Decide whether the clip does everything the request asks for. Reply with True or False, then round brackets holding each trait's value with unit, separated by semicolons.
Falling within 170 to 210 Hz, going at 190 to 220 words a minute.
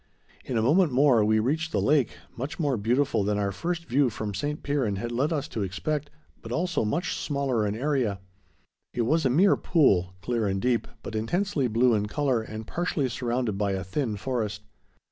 False (125 Hz; 195 wpm)